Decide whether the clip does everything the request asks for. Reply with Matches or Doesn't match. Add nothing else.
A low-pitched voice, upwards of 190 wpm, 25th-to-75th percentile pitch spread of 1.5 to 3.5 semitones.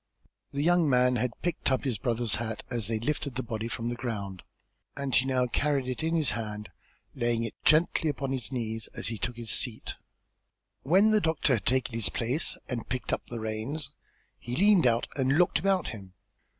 Doesn't match